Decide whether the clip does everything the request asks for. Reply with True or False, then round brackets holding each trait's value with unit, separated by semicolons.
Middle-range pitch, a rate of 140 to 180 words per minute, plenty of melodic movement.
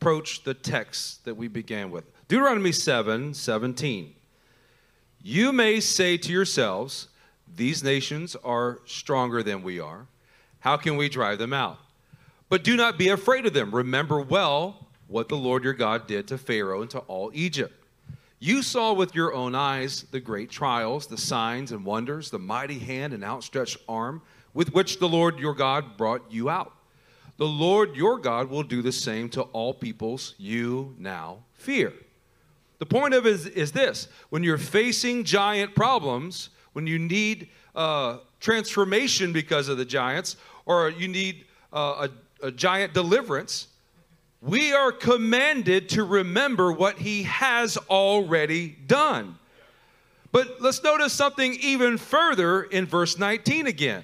True (160 Hz; 155 wpm; 7.5 semitones)